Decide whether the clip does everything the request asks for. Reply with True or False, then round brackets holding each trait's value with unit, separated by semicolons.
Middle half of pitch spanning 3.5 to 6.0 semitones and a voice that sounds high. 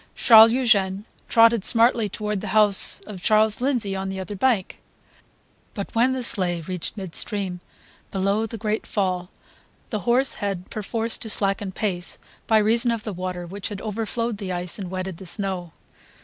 False (3.1 semitones; 205 Hz)